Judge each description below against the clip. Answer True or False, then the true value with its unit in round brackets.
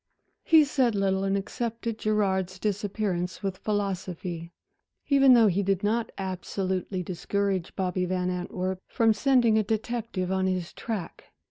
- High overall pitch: True (195 Hz)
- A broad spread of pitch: False (2.9 semitones)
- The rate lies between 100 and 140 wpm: True (135 wpm)